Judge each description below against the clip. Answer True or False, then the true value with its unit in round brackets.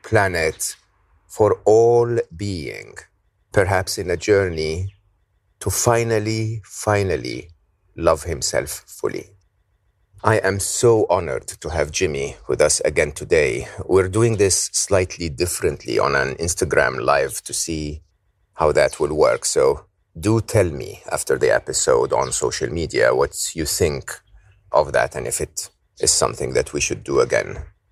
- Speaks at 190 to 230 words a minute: False (140 wpm)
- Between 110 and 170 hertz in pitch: False (100 Hz)